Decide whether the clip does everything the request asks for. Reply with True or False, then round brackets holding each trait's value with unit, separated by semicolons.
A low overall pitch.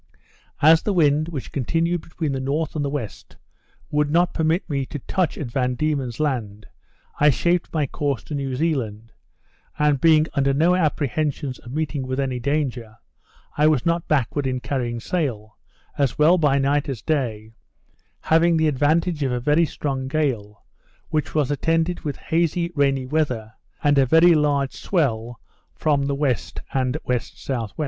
False (145 Hz)